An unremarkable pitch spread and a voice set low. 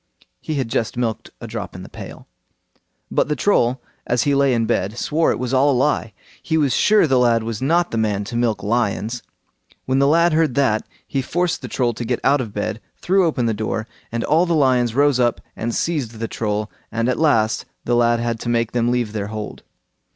Yes: average, 3.8 semitones; low, 120 Hz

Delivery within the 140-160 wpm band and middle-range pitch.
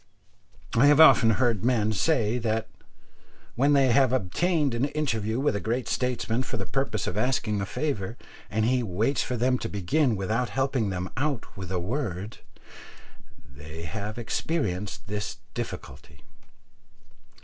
No: average, 150 wpm; low, 115 Hz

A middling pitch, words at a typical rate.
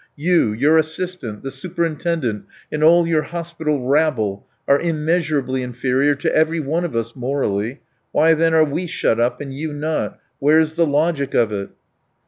Yes: medium, 150 Hz; average, 160 wpm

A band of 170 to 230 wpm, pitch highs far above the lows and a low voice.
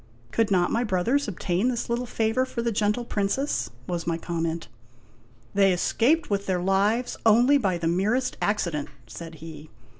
No: average, 180 wpm; wide, 5.7 semitones; high, 200 Hz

